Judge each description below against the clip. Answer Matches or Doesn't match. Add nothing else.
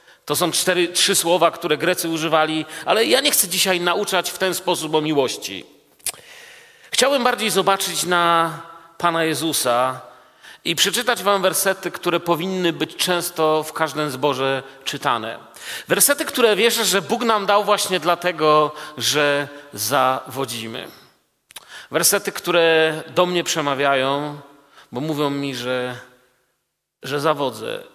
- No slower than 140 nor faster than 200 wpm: Doesn't match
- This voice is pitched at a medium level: Matches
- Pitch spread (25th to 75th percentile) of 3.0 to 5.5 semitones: Matches